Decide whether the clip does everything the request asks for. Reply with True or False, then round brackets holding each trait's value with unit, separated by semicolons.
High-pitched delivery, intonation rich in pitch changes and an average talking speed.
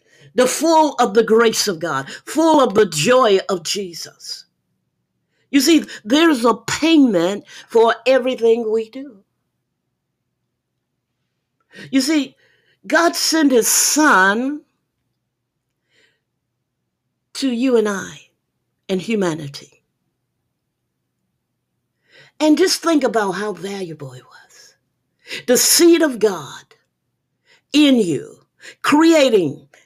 False (245 Hz; 6.6 semitones; 100 wpm)